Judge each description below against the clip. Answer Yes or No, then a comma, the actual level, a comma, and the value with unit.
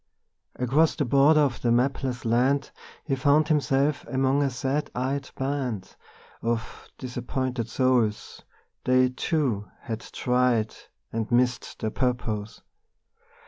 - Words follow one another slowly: Yes, slow, 115 wpm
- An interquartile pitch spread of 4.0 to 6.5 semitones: No, narrow, 2.6 semitones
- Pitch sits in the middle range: No, low, 130 Hz